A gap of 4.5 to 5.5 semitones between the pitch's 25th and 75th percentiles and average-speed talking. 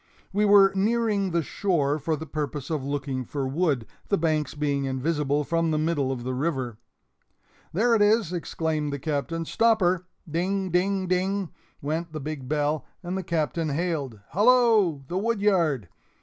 Yes: average, 4.8 semitones; average, 165 wpm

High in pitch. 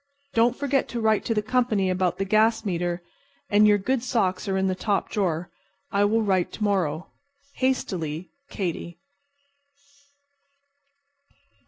Yes: high, 200 Hz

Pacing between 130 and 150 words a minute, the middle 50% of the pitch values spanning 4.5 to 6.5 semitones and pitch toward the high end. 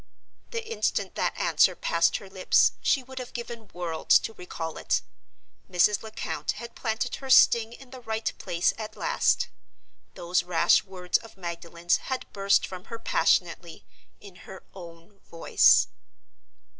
Yes: average, 145 wpm; average, 4.9 semitones; high, 195 Hz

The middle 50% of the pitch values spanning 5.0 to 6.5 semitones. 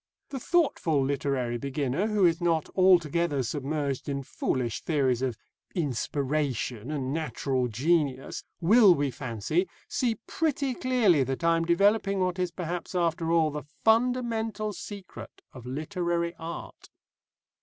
Yes: wide, 5.4 semitones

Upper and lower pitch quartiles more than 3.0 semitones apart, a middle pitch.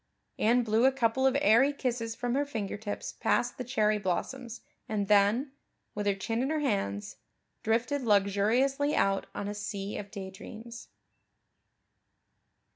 No: average, 4.0 semitones; high, 225 Hz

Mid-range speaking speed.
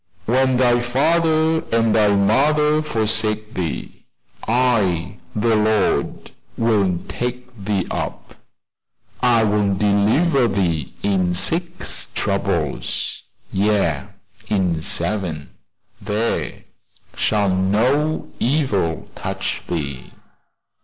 No: slow, 90 wpm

